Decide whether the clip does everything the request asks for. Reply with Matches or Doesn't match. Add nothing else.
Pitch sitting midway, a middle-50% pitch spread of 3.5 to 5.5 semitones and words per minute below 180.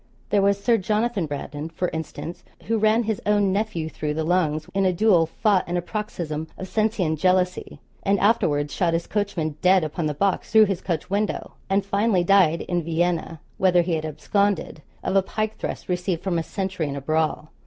Doesn't match